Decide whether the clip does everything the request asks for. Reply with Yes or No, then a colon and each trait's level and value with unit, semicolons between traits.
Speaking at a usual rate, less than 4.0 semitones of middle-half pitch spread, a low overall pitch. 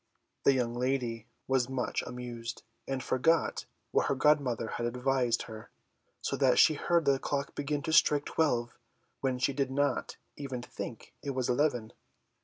Yes: average, 160 wpm; narrow, 2.6 semitones; low, 130 Hz